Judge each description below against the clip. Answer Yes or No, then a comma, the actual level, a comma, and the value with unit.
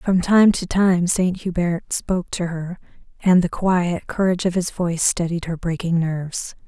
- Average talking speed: Yes, average, 180 wpm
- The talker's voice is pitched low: No, medium, 175 Hz